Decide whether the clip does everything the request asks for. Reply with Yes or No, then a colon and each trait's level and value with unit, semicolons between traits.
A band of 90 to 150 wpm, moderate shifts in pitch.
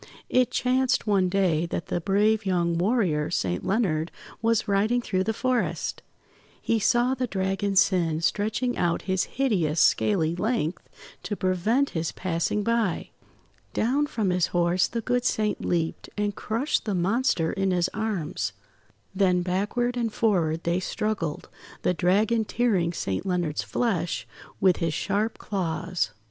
Yes: average, 145 wpm; average, 4.4 semitones